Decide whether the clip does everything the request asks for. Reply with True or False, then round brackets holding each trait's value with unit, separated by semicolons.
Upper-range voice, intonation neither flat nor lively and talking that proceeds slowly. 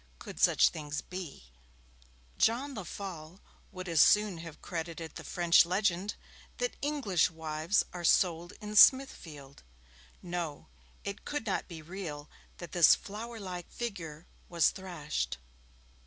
False (175 Hz; 3.8 semitones; 125 wpm)